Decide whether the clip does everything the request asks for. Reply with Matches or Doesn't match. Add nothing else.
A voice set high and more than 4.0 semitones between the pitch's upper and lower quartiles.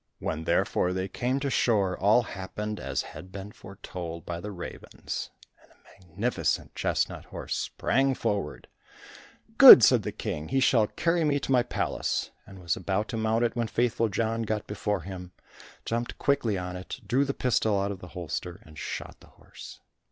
Doesn't match